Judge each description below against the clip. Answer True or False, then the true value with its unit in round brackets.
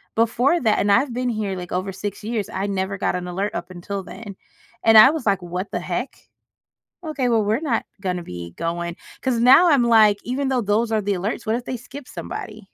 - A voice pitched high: True (210 Hz)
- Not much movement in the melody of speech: False (4.3 semitones)